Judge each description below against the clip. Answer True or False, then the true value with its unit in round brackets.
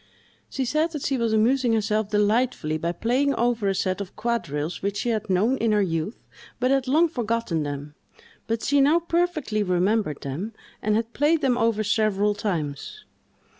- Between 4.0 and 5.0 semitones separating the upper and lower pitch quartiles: True (4.7 semitones)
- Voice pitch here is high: True (220 Hz)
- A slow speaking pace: False (175 wpm)